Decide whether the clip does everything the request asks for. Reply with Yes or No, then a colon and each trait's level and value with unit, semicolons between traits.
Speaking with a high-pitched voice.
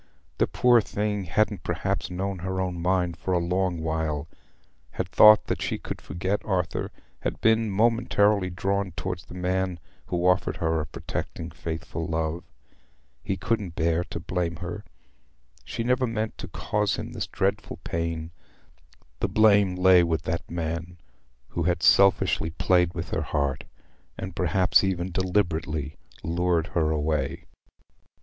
No: very low, 90 Hz